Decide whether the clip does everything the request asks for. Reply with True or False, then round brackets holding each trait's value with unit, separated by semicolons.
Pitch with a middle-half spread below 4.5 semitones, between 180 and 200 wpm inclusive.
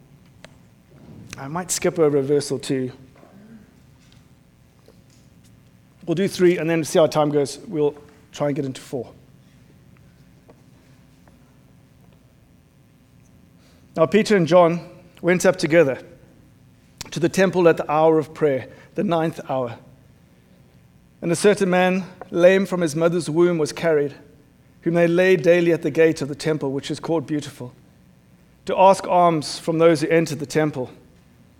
False (3.3 semitones; 140 wpm)